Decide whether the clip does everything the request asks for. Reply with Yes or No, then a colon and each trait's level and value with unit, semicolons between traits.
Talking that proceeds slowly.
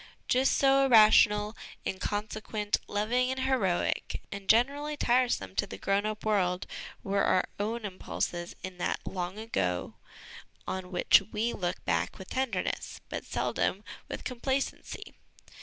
Yes: slow, 130 wpm